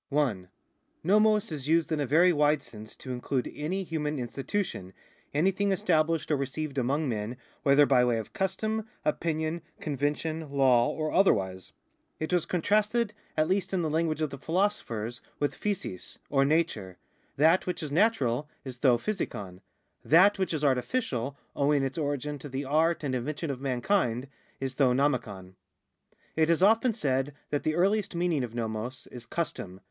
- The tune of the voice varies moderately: Yes, average, 4.9 semitones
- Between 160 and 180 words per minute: Yes, average, 165 wpm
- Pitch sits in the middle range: Yes, medium, 150 Hz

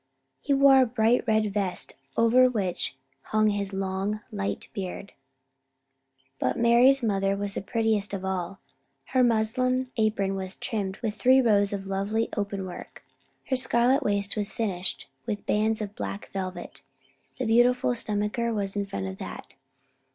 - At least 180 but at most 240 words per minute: No, average, 155 wpm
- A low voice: No, high, 210 Hz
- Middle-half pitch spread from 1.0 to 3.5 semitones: Yes, average, 3.2 semitones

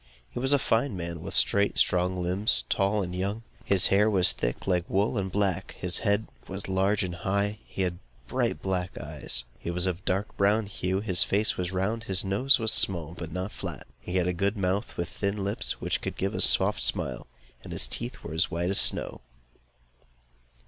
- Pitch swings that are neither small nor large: No, narrow, 2.3 semitones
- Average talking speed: No, fast, 215 wpm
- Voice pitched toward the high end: No, very low, 95 Hz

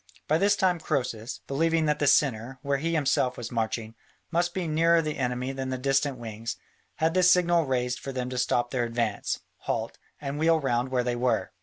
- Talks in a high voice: No, low, 135 Hz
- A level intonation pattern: No, average, 4.6 semitones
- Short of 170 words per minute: No, average, 200 wpm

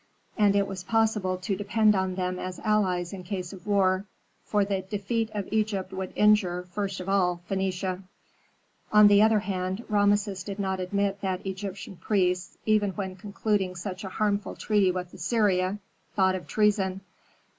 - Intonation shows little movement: Yes, narrow, 1.9 semitones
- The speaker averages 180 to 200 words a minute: No, average, 165 wpm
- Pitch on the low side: No, high, 195 Hz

